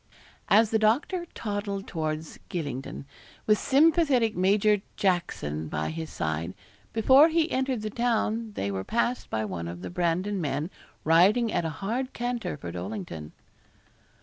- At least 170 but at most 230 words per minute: No, average, 145 wpm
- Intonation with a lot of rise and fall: Yes, wide, 8.9 semitones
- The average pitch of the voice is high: Yes, high, 195 Hz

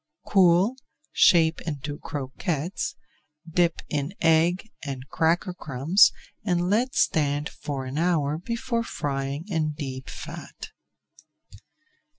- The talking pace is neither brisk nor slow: No, slow, 105 wpm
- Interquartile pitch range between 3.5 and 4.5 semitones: Yes, average, 3.9 semitones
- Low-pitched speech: No, medium, 160 Hz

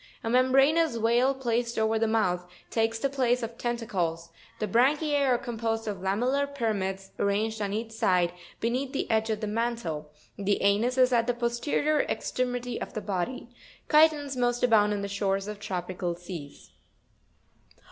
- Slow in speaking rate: No, average, 165 wpm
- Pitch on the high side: Yes, high, 225 Hz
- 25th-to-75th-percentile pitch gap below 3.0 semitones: No, average, 3.8 semitones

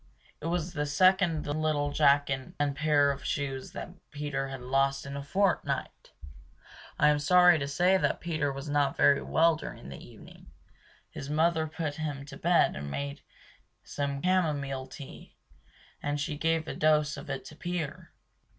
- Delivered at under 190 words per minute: Yes, average, 165 wpm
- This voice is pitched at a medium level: Yes, medium, 145 Hz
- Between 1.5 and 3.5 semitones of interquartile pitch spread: Yes, narrow, 2.4 semitones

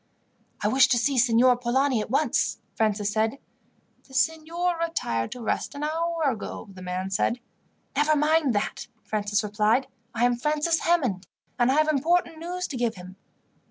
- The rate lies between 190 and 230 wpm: No, average, 165 wpm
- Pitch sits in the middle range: No, very high, 255 Hz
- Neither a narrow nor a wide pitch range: No, wide, 6.2 semitones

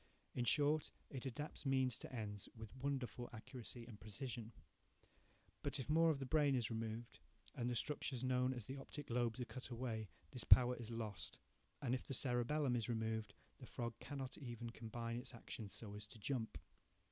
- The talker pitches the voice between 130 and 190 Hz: No, low, 120 Hz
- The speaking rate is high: No, average, 185 wpm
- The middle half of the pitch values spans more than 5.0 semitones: No, average, 2.9 semitones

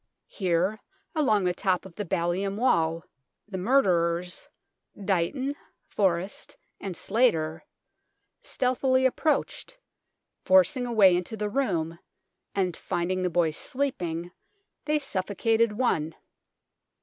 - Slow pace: Yes, slow, 105 wpm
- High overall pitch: Yes, high, 195 Hz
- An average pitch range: No, wide, 6.3 semitones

